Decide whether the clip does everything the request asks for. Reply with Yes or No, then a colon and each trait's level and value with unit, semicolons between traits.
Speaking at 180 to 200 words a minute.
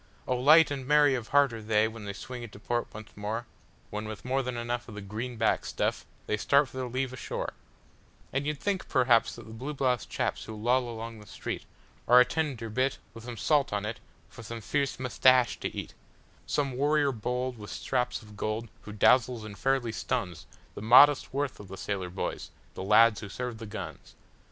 Yes: average, 195 wpm